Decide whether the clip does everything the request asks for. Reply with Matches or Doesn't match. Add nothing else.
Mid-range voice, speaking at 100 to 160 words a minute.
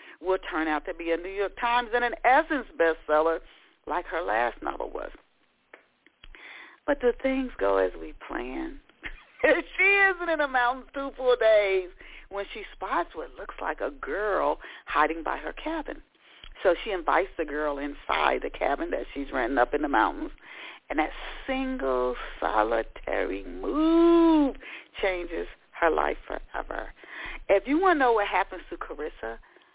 Doesn't match